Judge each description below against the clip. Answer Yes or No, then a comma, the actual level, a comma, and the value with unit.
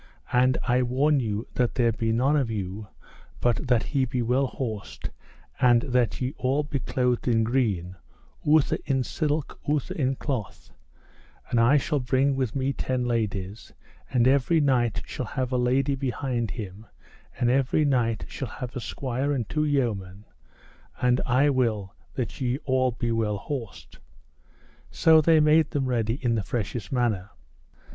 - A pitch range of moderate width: Yes, average, 3.0 semitones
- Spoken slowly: No, average, 160 wpm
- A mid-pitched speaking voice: No, low, 125 Hz